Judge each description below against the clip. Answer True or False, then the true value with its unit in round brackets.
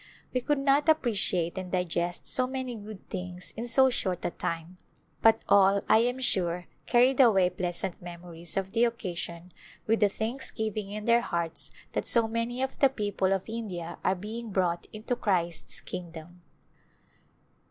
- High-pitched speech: True (200 Hz)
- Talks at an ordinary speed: True (160 wpm)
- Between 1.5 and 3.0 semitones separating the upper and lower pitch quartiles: False (4.8 semitones)